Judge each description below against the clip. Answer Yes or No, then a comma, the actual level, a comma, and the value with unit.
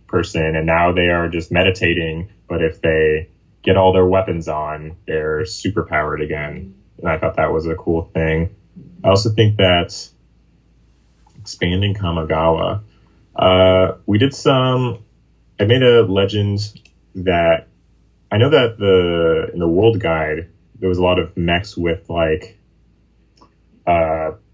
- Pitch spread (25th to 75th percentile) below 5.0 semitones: Yes, average, 3.4 semitones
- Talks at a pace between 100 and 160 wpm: Yes, average, 140 wpm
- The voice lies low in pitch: Yes, very low, 90 Hz